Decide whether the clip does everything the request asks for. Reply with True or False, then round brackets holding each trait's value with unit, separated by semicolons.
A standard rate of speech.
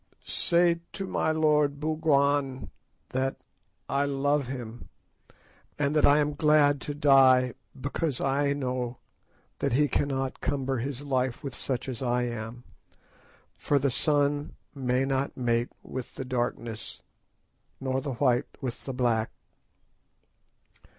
False (125 wpm)